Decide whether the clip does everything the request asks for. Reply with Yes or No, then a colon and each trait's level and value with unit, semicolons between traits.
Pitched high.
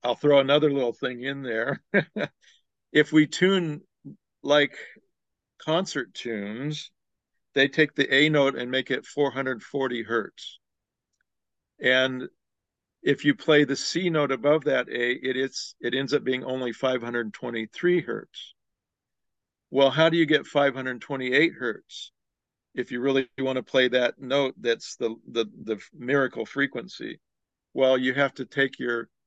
No: low, 135 Hz